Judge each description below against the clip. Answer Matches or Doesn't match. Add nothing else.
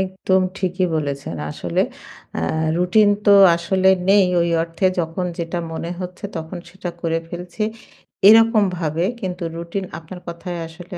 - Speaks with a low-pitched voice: Doesn't match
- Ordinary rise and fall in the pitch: Doesn't match